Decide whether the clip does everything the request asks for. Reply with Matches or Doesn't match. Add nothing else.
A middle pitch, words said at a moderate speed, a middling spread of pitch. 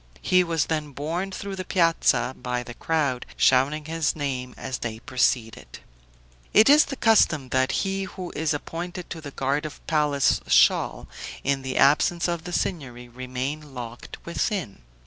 Matches